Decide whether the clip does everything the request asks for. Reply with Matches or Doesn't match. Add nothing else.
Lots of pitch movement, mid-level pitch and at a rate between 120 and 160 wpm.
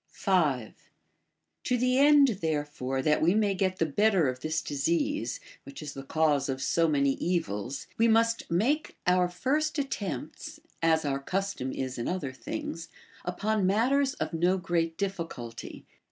Matches